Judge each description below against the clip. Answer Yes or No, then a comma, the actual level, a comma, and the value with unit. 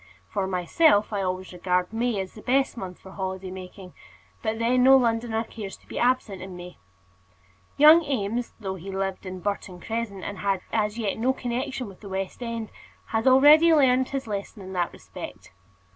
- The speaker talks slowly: No, average, 185 wpm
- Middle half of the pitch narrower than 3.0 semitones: No, average, 4.4 semitones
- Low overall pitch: No, high, 210 Hz